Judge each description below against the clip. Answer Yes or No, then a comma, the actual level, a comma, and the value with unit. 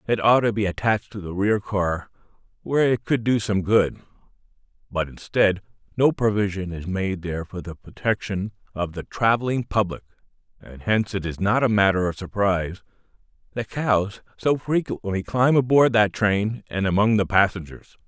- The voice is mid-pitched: No, low, 100 Hz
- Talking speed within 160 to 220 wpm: Yes, average, 165 wpm